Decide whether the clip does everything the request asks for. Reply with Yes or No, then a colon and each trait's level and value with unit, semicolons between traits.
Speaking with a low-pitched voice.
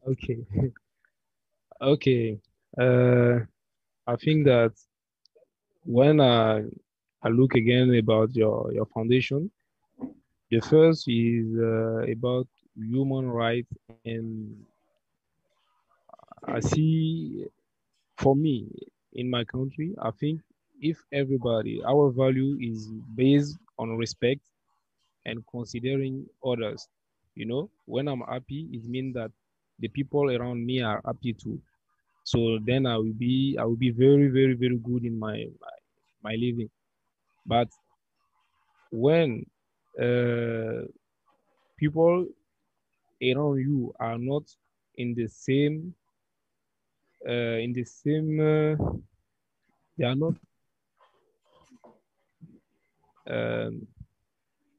Yes: low, 125 Hz